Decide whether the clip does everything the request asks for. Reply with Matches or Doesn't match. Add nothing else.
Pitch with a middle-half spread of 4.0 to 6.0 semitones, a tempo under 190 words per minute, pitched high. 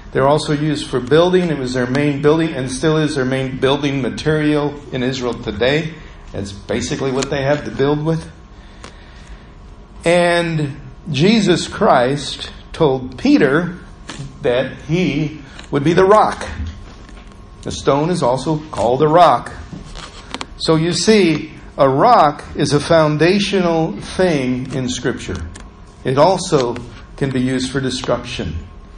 Doesn't match